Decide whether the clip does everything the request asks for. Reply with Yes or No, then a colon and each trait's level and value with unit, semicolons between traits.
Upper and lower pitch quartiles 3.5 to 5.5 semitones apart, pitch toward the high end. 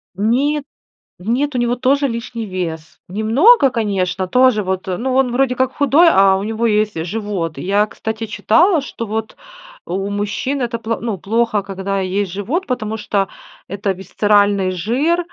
Yes: average, 4.4 semitones; high, 220 Hz